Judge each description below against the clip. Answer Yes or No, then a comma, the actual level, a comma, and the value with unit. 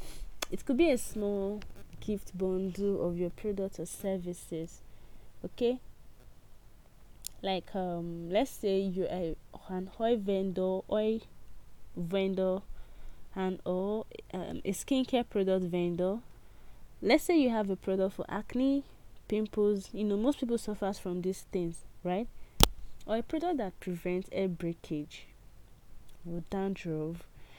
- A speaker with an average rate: No, slow, 125 wpm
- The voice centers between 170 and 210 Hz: Yes, high, 190 Hz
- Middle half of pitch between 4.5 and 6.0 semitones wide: No, average, 3.0 semitones